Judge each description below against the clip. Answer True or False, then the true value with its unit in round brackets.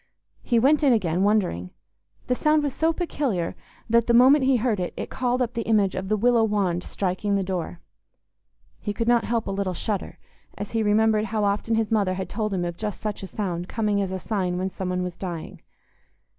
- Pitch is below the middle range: False (210 Hz)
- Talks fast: True (215 wpm)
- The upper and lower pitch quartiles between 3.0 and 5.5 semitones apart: True (3.7 semitones)